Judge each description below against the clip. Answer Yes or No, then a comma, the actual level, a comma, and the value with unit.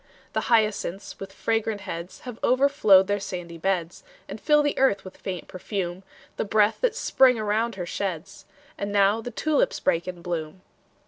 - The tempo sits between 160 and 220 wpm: Yes, average, 170 wpm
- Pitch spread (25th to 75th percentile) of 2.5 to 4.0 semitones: Yes, average, 3.7 semitones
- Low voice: No, high, 200 Hz